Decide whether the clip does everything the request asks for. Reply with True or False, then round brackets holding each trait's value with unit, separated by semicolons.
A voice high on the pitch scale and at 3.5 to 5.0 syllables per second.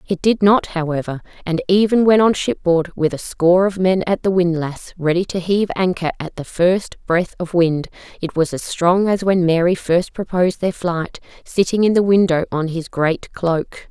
False (180 Hz; 4.8 syllables/s)